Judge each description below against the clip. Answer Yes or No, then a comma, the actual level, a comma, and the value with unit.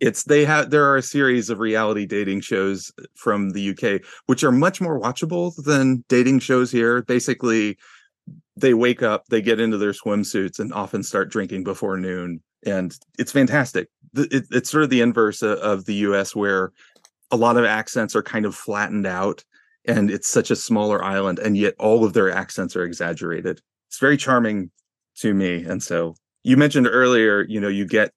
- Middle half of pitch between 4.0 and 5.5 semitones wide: Yes, average, 4.4 semitones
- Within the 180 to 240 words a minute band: Yes, average, 185 wpm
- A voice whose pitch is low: Yes, low, 110 Hz